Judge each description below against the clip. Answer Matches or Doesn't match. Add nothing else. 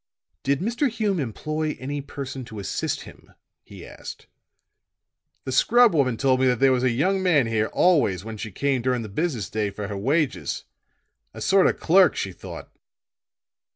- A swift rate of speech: Doesn't match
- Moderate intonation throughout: Doesn't match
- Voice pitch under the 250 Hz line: Matches